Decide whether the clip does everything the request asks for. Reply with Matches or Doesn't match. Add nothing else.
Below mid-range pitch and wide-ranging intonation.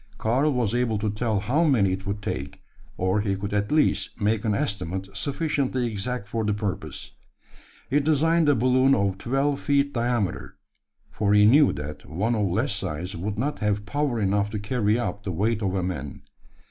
Doesn't match